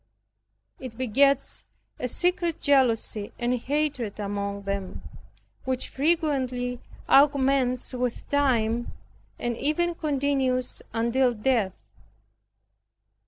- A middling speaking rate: No, slow, 85 wpm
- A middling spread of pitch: Yes, average, 3.4 semitones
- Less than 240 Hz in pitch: No, very high, 255 Hz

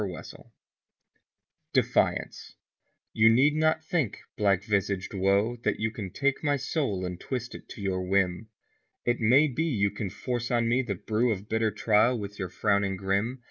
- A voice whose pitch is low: Yes, low, 110 Hz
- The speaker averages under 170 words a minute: No, average, 175 wpm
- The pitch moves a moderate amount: Yes, average, 3.9 semitones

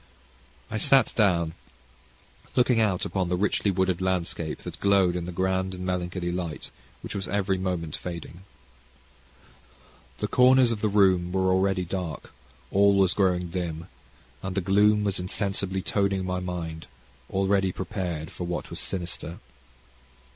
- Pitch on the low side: Yes, very low, 95 Hz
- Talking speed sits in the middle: Yes, average, 145 wpm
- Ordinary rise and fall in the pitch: No, narrow, 1.9 semitones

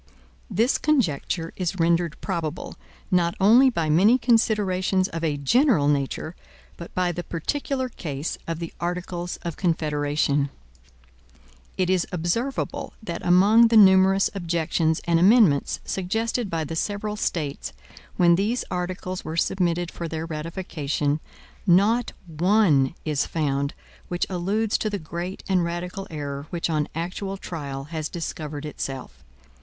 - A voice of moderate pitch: Yes, medium, 175 Hz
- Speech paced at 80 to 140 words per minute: Yes, slow, 135 wpm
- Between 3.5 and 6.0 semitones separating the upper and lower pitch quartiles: Yes, average, 3.8 semitones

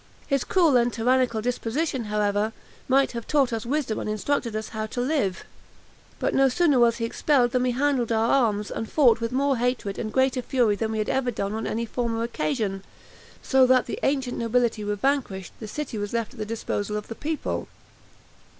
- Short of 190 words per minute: No, average, 200 wpm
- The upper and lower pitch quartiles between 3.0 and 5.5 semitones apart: Yes, average, 3.4 semitones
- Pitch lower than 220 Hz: No, high, 235 Hz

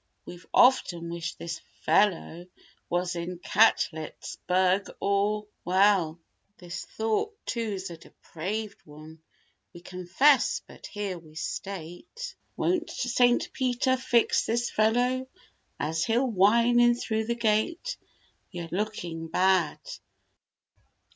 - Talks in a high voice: Yes, high, 200 Hz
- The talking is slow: Yes, slow, 110 wpm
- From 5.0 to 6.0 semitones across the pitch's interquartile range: Yes, wide, 5.5 semitones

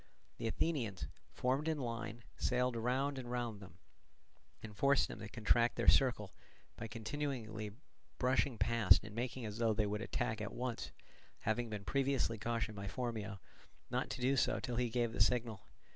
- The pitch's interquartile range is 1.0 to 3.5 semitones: Yes, average, 2.7 semitones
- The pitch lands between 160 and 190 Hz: No, low, 115 Hz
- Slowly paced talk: No, average, 170 wpm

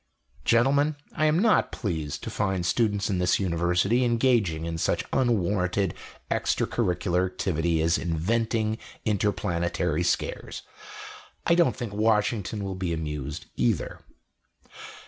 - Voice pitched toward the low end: Yes, very low, 95 Hz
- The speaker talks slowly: Yes, slow, 120 wpm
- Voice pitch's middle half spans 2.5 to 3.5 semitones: No, average, 4.9 semitones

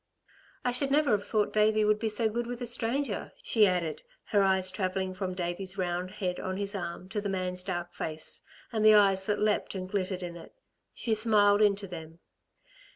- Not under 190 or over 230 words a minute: Yes, average, 200 wpm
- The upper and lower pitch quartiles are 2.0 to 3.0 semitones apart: Yes, narrow, 2.6 semitones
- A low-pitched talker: No, high, 200 Hz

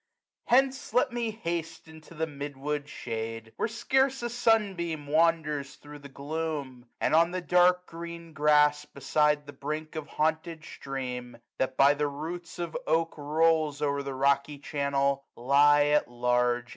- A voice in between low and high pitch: Yes, medium, 150 Hz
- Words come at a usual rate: Yes, average, 160 wpm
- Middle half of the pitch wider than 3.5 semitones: No, average, 3.2 semitones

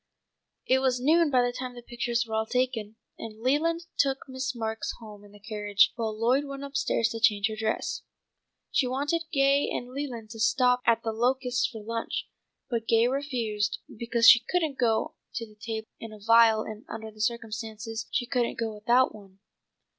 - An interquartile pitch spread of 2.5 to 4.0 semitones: Yes, average, 2.8 semitones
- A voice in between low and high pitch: No, high, 235 Hz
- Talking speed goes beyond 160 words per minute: Yes, average, 190 wpm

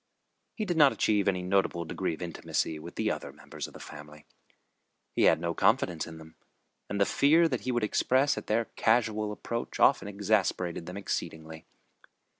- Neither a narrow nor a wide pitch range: No, wide, 5.8 semitones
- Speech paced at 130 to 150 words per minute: No, average, 180 wpm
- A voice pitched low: Yes, low, 100 Hz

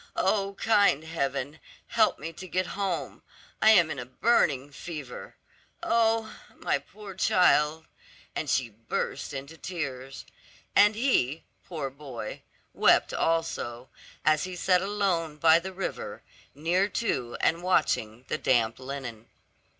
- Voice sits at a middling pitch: Yes, medium, 160 Hz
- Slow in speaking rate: Yes, slow, 130 wpm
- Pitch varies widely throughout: Yes, wide, 5.8 semitones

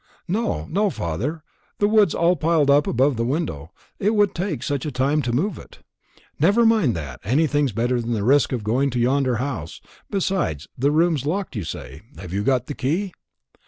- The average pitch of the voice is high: No, medium, 140 Hz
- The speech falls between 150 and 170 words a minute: No, average, 195 wpm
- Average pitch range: No, wide, 6.3 semitones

